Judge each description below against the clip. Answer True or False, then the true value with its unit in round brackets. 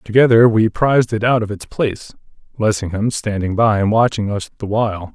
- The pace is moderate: True (175 wpm)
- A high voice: False (110 Hz)